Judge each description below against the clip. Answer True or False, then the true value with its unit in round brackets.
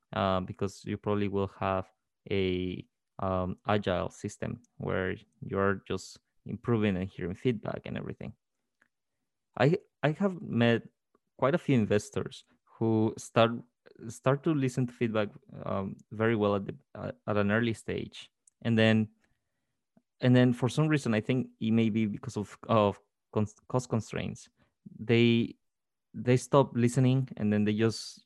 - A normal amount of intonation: True (3.4 semitones)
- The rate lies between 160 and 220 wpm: False (150 wpm)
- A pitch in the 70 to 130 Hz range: True (110 Hz)